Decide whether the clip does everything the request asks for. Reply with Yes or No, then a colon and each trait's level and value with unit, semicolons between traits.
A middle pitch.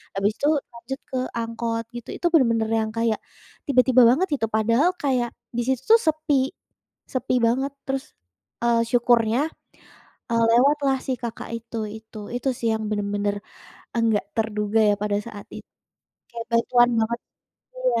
No: high, 235 Hz